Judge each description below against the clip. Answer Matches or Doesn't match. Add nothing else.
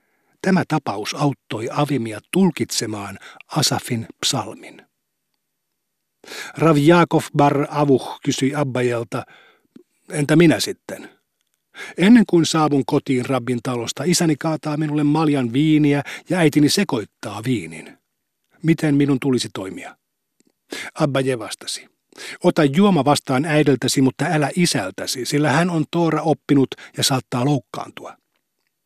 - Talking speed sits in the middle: Matches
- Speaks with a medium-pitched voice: Matches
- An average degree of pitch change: Matches